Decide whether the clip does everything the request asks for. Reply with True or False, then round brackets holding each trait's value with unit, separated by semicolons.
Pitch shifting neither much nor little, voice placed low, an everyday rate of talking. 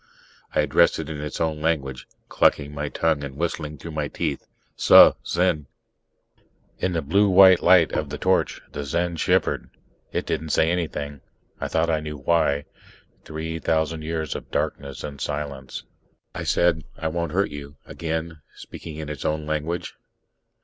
False (2.3 semitones; 80 Hz; 165 wpm)